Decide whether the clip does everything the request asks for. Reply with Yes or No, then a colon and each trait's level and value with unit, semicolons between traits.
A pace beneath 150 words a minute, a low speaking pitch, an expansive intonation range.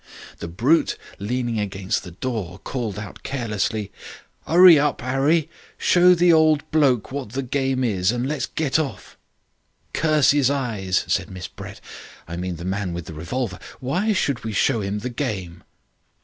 No: average, 165 wpm; low, 120 Hz; wide, 6.6 semitones